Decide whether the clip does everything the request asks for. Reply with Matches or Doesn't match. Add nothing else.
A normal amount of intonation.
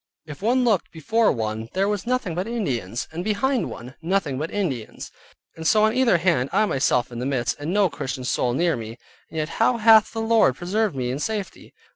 Doesn't match